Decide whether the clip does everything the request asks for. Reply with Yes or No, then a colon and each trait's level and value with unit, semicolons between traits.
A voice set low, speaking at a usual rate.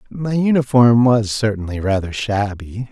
No: low, 115 Hz; slow, 125 wpm